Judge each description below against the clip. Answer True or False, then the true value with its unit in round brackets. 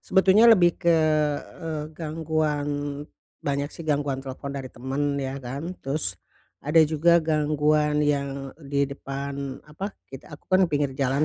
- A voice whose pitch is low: False (145 Hz)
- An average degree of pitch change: False (2.1 semitones)